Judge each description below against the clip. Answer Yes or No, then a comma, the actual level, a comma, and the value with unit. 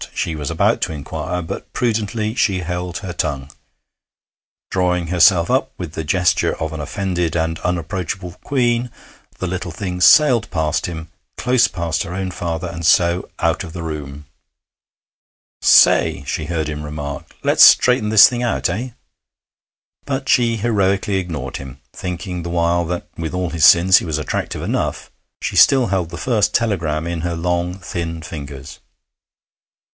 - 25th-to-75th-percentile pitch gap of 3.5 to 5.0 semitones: No, average, 3.1 semitones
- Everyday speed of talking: Yes, average, 160 wpm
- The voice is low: Yes, very low, 90 Hz